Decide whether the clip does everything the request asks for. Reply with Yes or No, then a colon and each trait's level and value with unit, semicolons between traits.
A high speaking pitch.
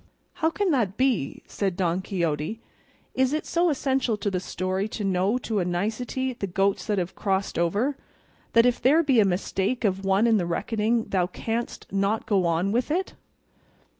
Yes: high, 205 Hz